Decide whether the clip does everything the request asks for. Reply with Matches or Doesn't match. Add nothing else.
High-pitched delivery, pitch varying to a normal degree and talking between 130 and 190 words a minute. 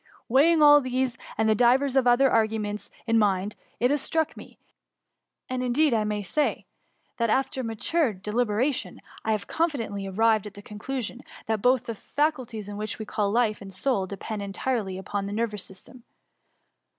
Matches